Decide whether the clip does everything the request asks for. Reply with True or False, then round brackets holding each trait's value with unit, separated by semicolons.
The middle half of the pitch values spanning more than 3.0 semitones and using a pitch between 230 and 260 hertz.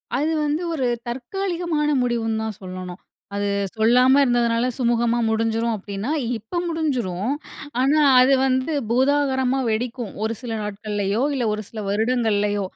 True (3.4 semitones; 235 Hz)